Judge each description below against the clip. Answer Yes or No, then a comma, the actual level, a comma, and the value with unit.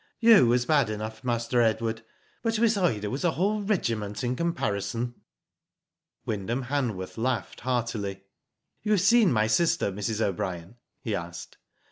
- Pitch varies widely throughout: Yes, wide, 7.5 semitones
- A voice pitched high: No, low, 120 Hz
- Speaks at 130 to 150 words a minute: Yes, average, 140 wpm